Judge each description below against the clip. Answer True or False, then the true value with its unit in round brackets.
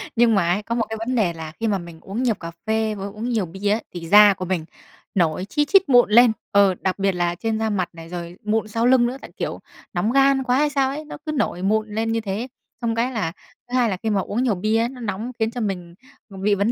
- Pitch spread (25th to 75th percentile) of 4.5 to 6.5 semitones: False (3.8 semitones)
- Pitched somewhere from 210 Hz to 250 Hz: True (215 Hz)